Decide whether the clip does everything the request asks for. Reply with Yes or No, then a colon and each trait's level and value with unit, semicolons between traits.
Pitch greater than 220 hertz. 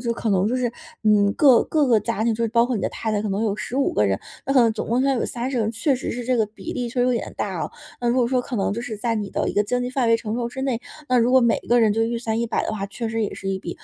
Yes: high, 230 Hz